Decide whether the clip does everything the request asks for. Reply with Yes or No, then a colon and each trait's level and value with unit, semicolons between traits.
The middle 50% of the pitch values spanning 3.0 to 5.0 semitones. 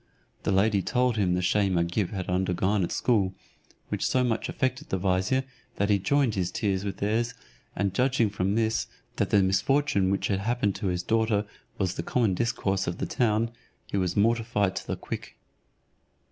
Yes: average, 3.5 semitones